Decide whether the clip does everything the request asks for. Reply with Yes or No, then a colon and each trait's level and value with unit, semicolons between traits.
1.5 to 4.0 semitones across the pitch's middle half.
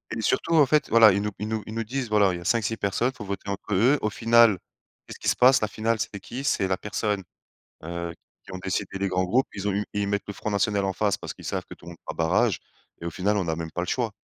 Yes: average, 3.1 semitones